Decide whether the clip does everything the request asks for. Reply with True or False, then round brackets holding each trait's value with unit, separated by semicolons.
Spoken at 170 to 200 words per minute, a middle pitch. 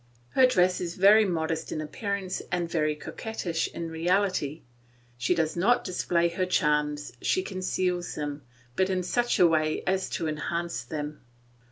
False (155 wpm; 170 Hz)